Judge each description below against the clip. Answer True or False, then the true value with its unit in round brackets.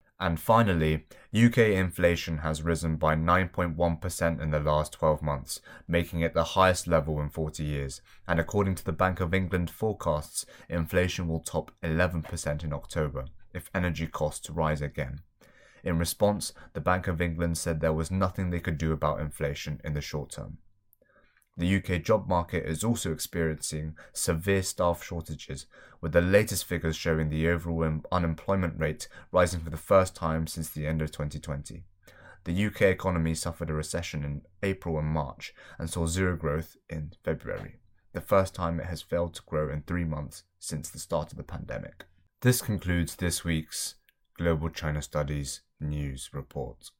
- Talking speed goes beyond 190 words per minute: False (165 wpm)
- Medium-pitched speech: False (85 Hz)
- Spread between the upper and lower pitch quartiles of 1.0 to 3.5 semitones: True (2.7 semitones)